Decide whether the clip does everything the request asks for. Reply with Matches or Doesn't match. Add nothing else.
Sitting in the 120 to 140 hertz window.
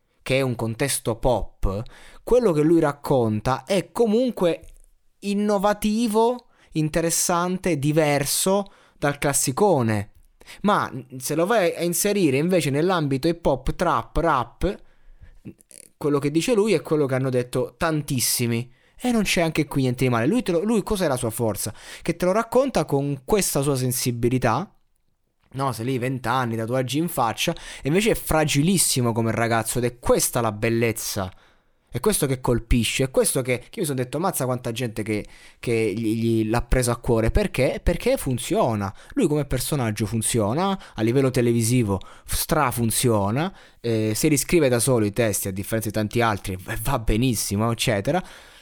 Matches